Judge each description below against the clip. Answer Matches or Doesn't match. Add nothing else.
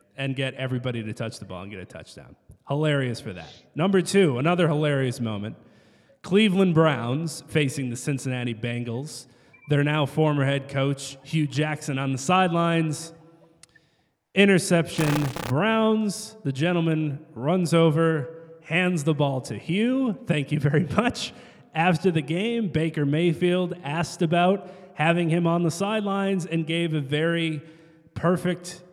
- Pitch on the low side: Doesn't match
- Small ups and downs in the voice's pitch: Doesn't match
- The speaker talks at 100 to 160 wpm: Matches